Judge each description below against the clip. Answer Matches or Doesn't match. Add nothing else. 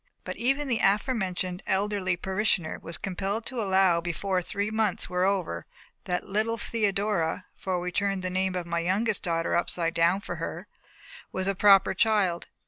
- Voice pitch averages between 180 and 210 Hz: Matches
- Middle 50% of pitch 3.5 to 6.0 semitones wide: Doesn't match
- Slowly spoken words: Doesn't match